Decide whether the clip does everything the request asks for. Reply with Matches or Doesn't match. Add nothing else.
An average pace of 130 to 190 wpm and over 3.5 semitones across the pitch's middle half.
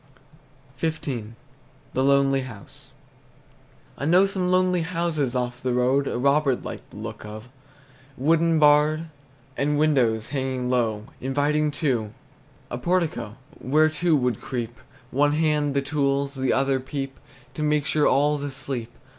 Doesn't match